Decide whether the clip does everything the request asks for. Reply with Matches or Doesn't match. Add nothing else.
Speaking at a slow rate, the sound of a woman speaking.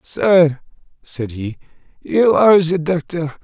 Doesn't match